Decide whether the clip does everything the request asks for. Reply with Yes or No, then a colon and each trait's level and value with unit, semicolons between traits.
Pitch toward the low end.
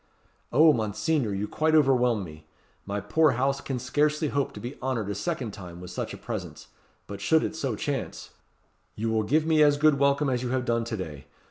Yes: low, 125 Hz